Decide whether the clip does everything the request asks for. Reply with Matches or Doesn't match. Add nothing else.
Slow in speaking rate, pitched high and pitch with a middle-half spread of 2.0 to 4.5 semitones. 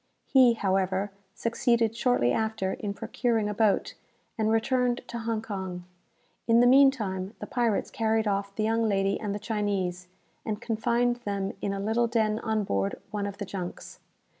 Doesn't match